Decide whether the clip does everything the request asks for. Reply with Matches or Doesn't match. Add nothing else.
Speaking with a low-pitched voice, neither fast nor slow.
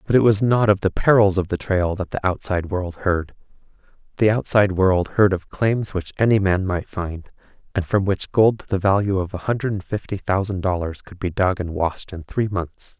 Doesn't match